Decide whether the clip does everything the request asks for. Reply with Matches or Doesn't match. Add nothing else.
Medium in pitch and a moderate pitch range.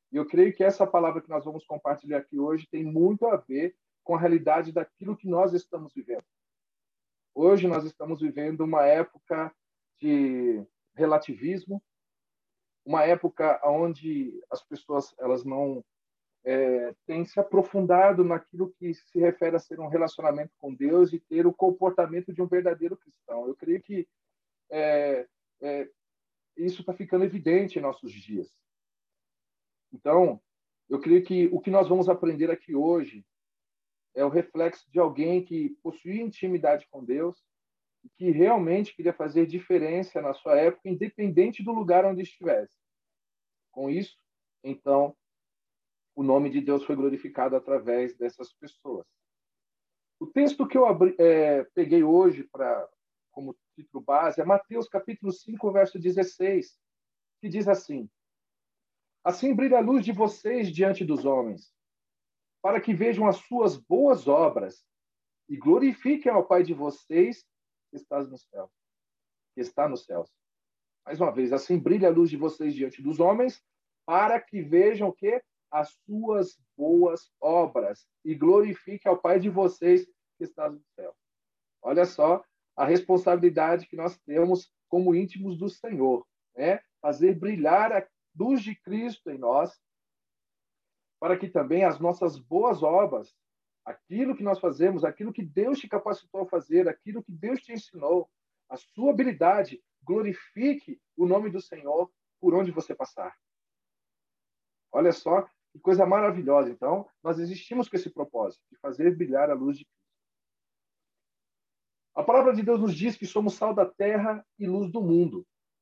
Matches